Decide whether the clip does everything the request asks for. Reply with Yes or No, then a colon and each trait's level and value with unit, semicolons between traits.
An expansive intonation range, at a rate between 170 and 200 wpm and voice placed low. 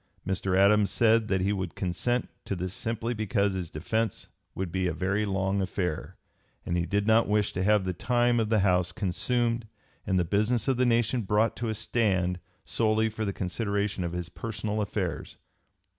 No: average, 3.2 semitones; average, 190 wpm; low, 100 Hz